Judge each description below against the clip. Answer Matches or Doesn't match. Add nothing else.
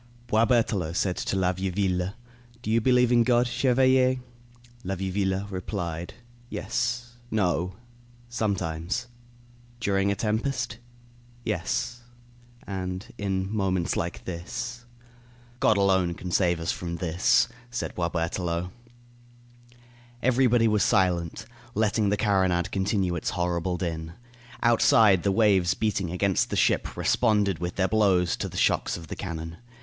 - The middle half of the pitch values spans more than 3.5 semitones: Matches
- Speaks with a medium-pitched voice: Doesn't match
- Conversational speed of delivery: Doesn't match